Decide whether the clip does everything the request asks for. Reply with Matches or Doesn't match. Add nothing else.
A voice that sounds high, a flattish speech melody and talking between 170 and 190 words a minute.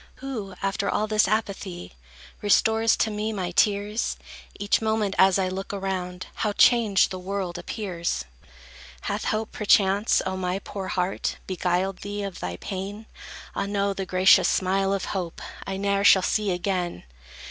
Doesn't match